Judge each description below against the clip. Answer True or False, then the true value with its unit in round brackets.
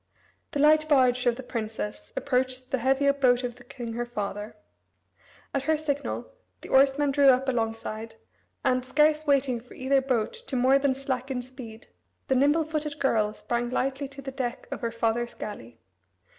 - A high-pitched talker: True (260 Hz)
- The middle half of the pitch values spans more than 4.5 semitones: False (2.7 semitones)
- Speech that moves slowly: False (170 wpm)